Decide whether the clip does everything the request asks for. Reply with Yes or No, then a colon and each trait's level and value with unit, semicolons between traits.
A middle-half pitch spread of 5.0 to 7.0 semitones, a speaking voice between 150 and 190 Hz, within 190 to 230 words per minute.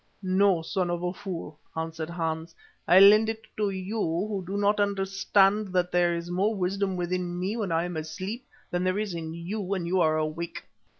No: average, 2.8 semitones; medium, 185 Hz; average, 195 wpm